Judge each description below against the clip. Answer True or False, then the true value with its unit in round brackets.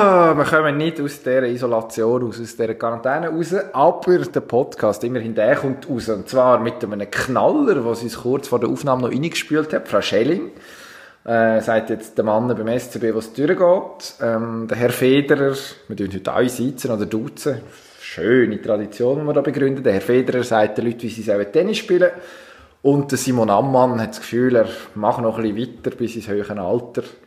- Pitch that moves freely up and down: False (3.5 semitones)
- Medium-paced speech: False (195 wpm)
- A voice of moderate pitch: False (120 Hz)